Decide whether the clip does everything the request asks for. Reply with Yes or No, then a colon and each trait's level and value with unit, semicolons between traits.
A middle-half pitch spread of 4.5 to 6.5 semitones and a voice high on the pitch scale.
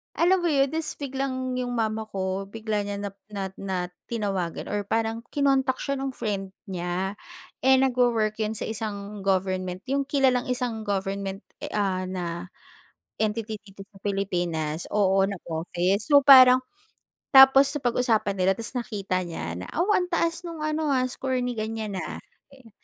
Yes: average, 5.3 semitones; high, 220 Hz